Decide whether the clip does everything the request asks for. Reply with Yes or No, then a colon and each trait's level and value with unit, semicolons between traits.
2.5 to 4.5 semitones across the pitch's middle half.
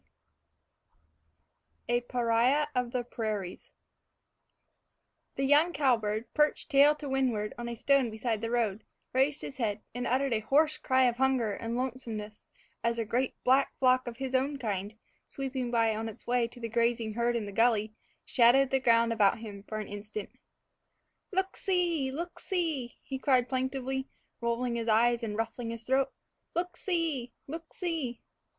Yes: average, 2.9 semitones